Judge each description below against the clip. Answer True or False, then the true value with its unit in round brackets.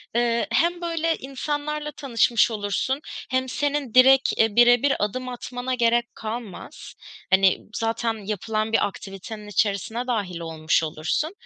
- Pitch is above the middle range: True (235 Hz)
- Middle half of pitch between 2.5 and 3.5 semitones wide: False (4.1 semitones)